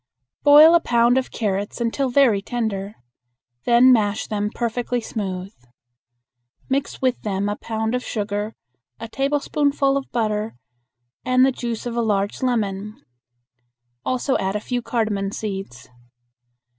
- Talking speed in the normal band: No, slow, 130 wpm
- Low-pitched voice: No, high, 230 Hz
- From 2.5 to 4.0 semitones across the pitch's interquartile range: Yes, average, 3.6 semitones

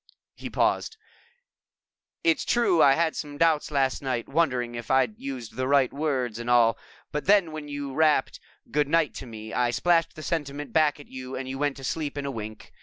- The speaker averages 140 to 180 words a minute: No, average, 195 wpm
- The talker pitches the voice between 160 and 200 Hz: No, medium, 140 Hz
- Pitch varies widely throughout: No, average, 3.5 semitones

